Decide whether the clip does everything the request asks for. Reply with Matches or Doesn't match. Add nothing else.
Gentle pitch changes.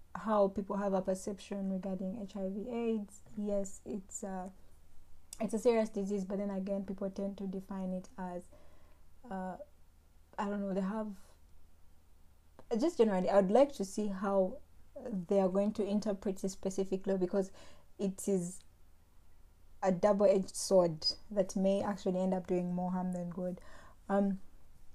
Matches